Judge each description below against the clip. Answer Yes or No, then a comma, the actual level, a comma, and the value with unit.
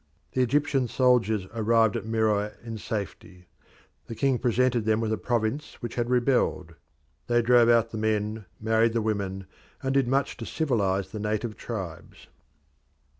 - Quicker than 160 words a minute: No, average, 155 wpm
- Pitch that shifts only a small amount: Yes, narrow, 2.3 semitones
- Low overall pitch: Yes, low, 115 Hz